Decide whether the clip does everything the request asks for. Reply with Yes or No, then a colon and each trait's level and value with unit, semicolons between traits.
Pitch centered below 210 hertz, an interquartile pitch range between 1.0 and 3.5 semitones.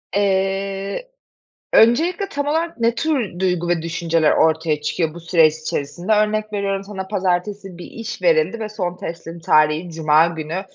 No: high, 190 Hz; average, 4.3 semitones